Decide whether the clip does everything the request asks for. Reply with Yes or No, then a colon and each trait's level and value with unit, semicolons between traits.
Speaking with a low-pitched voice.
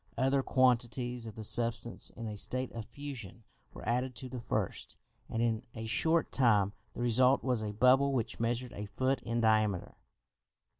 Yes: low, 120 Hz